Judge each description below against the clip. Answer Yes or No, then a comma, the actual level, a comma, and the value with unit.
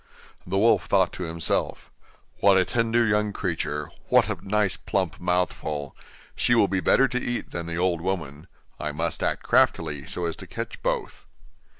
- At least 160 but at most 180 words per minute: Yes, average, 175 wpm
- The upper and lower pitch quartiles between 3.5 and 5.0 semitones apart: Yes, average, 4.1 semitones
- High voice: No, very low, 90 Hz